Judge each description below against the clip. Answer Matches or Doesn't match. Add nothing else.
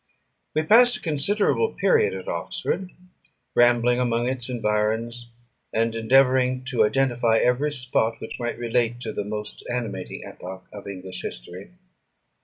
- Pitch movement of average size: Matches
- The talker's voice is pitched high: Doesn't match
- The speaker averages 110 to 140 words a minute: Matches